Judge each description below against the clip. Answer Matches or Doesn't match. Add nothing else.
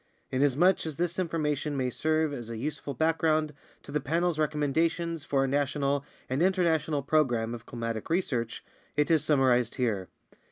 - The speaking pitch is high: Doesn't match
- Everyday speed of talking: Matches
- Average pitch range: Matches